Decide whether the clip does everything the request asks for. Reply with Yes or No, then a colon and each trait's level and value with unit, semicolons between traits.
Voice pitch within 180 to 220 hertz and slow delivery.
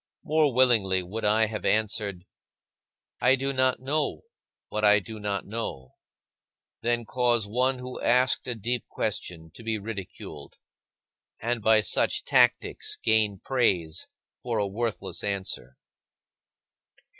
No: low, 110 Hz; slow, 125 wpm